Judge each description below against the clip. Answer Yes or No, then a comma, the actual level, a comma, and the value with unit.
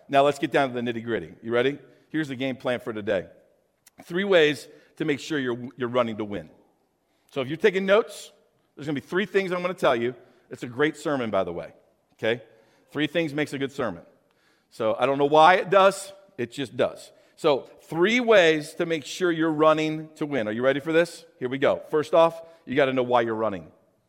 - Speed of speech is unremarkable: No, fast, 225 wpm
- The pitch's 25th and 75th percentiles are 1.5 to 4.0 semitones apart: No, average, 4.7 semitones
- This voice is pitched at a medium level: Yes, medium, 150 Hz